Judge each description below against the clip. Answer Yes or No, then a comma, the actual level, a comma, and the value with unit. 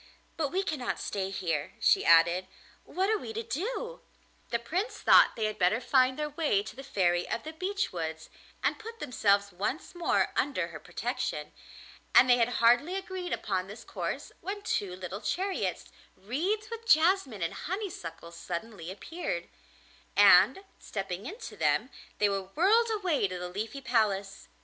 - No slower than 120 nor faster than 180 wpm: Yes, average, 165 wpm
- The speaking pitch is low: No, high, 240 Hz